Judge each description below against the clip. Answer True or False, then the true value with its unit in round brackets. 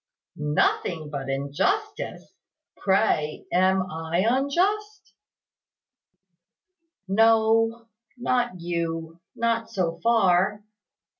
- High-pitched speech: True (195 Hz)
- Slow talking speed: True (70 wpm)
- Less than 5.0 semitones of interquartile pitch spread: False (5.6 semitones)